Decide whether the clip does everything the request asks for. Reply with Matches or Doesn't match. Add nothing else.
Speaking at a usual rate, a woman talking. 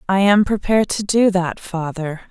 Matches